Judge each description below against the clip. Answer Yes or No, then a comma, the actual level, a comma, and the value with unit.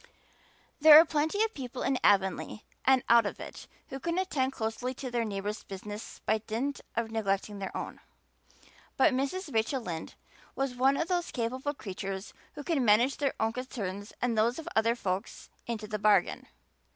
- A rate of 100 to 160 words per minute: No, average, 175 wpm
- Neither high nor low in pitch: No, high, 235 Hz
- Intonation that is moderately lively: Yes, average, 4.4 semitones